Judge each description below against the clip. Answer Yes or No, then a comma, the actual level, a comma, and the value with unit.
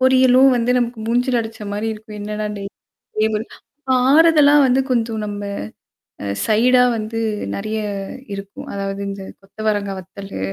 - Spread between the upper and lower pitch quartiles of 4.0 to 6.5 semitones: No, average, 3.6 semitones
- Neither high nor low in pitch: No, high, 220 Hz